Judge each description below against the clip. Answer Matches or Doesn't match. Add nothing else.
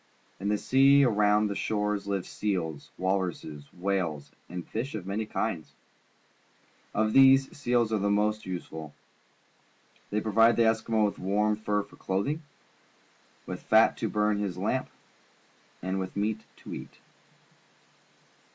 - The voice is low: Matches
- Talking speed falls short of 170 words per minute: Matches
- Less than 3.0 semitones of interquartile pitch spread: Matches